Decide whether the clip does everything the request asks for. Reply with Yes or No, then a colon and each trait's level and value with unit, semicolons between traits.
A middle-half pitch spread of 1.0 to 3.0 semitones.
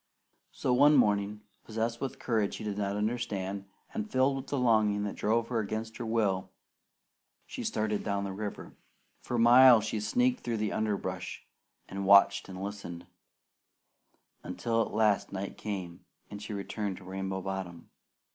Yes: average, 2.7 semitones